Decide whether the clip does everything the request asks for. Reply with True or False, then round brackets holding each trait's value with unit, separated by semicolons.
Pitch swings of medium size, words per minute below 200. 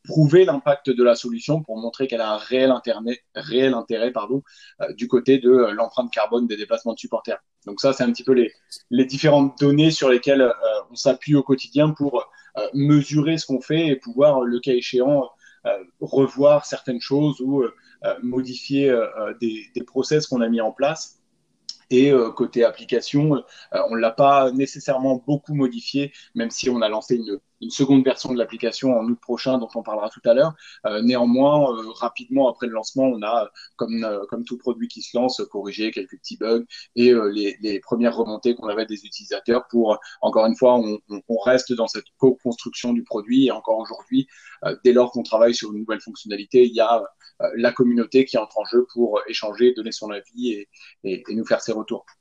False (3.2 semitones; 205 wpm)